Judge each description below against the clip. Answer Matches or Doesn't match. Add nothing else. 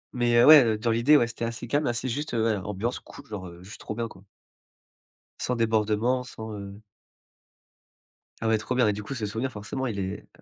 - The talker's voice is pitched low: Matches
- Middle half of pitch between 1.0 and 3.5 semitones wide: Matches